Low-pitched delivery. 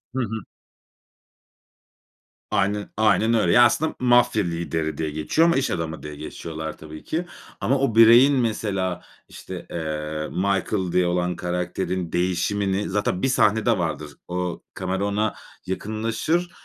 Yes: very low, 95 Hz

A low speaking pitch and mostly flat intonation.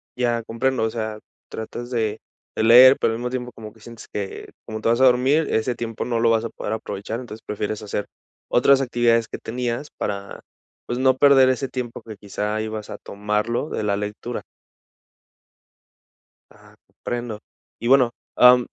Yes: low, 115 Hz; narrow, 2.3 semitones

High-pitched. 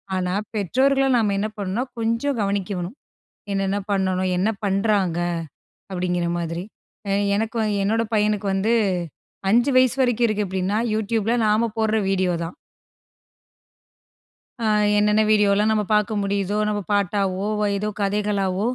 Yes: high, 205 Hz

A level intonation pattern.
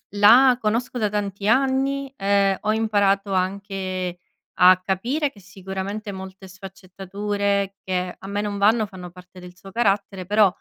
Yes: narrow, 2.0 semitones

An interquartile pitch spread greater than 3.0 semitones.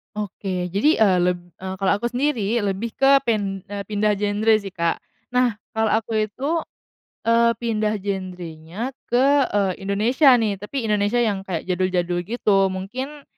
Yes: average, 3.4 semitones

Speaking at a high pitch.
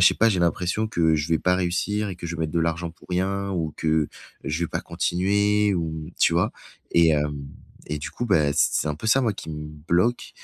No: very low, 85 Hz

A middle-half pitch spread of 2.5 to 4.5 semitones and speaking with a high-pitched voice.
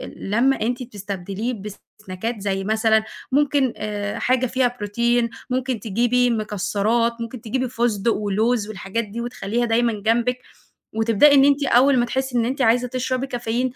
Yes: average, 2.8 semitones; high, 235 Hz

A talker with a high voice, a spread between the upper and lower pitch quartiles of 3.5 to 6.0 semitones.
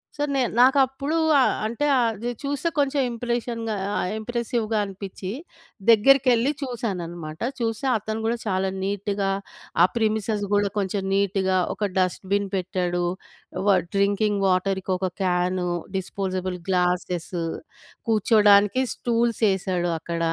Yes: high, 205 Hz; average, 3.8 semitones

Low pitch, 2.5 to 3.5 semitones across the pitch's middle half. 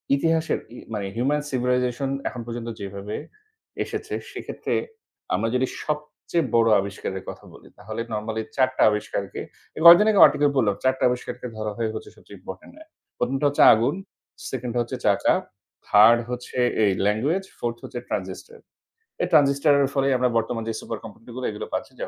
No: low, 120 Hz; average, 4.2 semitones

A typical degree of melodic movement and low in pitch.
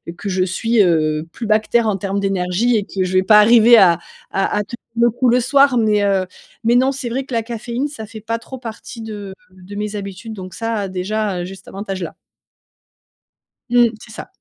No: average, 3.5 semitones; high, 215 Hz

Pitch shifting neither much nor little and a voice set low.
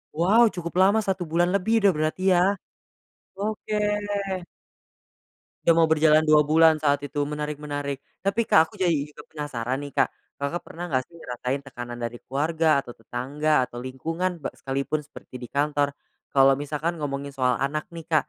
No: average, 3.5 semitones; medium, 150 Hz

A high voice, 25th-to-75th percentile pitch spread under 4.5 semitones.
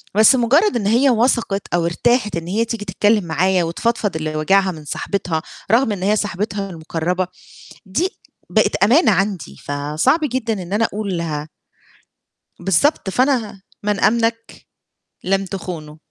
No: high, 200 Hz; average, 4.9 semitones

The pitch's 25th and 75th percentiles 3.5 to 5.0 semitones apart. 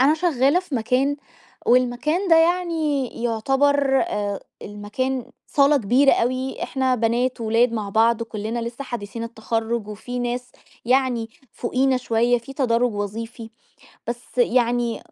No: average, 2.8 semitones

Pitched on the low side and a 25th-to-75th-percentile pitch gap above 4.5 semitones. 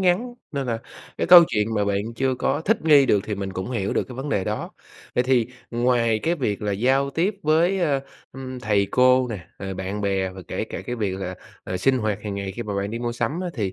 Yes: low, 120 Hz; average, 5.1 semitones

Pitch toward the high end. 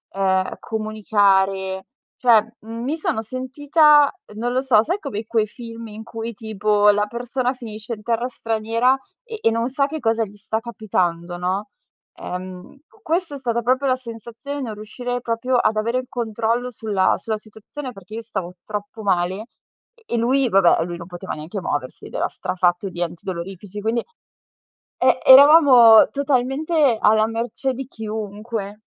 Yes: high, 225 Hz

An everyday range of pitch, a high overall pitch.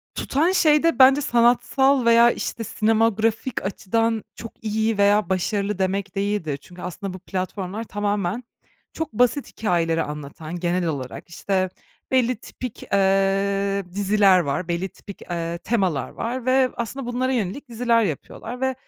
Yes: average, 4.3 semitones; high, 205 Hz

